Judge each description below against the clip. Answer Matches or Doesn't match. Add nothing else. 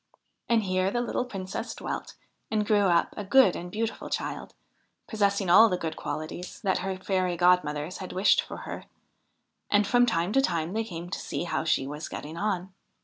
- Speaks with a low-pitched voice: Doesn't match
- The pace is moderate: Matches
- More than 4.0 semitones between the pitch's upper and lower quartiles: Doesn't match